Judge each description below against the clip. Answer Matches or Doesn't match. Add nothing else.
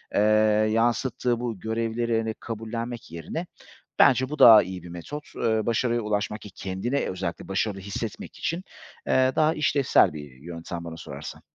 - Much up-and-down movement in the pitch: Doesn't match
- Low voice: Matches